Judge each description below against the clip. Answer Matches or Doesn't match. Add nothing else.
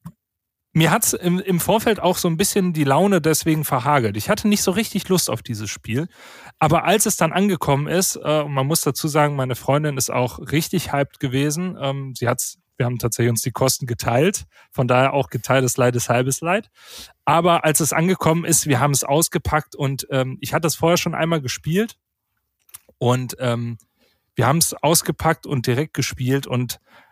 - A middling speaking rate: Doesn't match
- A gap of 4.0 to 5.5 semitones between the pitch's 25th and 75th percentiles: Matches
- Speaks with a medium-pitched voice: Matches